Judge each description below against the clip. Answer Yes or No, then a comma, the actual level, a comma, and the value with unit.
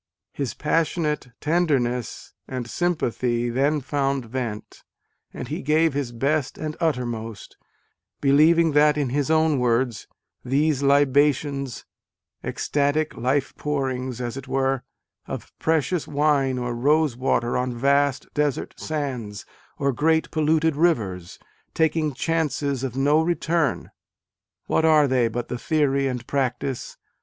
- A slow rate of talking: Yes, slow, 130 wpm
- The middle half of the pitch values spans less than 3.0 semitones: No, average, 3.4 semitones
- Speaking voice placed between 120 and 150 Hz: Yes, medium, 140 Hz